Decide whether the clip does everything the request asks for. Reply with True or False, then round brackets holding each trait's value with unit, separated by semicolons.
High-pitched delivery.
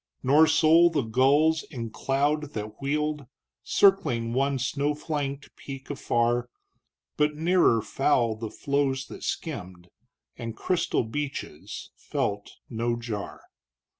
False (135 Hz)